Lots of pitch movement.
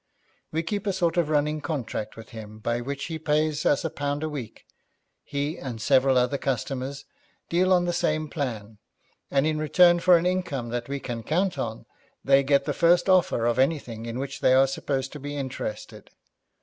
No: average, 4.1 semitones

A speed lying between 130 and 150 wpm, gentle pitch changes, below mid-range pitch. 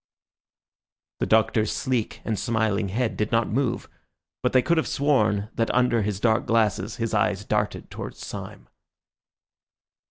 Yes: average, 140 wpm; narrow, 2.1 semitones; low, 110 Hz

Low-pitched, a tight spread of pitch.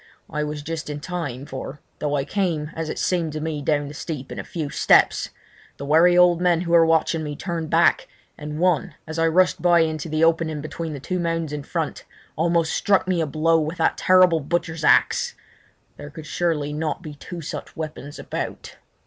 No: medium, 160 Hz; narrow, 2.3 semitones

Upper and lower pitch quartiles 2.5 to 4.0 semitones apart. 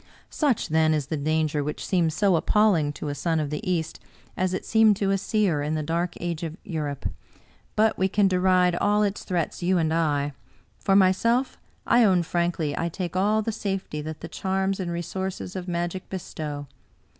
Yes: average, 3.6 semitones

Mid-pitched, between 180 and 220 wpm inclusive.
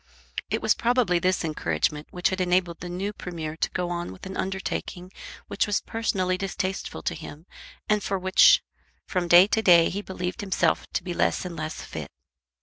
Yes: medium, 180 Hz; average, 185 wpm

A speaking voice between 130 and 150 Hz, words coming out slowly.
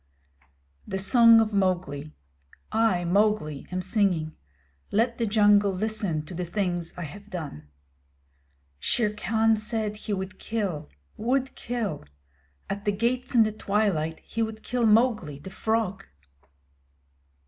No: high, 205 Hz; slow, 130 wpm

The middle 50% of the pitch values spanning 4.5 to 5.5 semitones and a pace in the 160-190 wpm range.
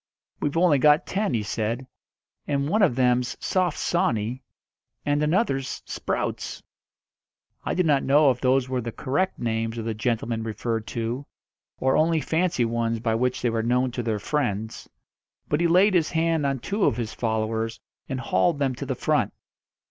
Yes: average, 4.8 semitones; average, 175 wpm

